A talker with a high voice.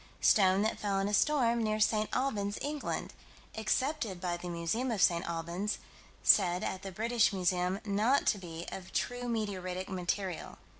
Yes: high, 200 Hz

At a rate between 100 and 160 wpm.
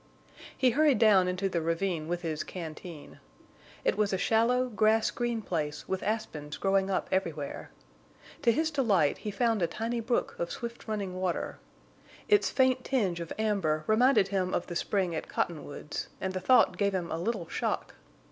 No: average, 175 wpm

